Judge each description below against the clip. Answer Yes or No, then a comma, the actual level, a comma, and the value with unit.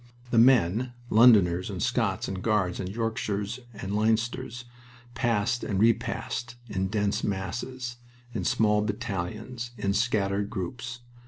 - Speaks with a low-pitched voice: Yes, low, 110 Hz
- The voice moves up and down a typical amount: Yes, average, 3.3 semitones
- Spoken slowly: Yes, slow, 120 wpm